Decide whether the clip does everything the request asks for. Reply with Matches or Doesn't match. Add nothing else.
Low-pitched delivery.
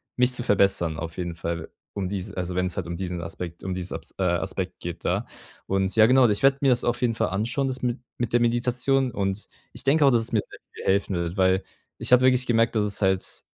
Matches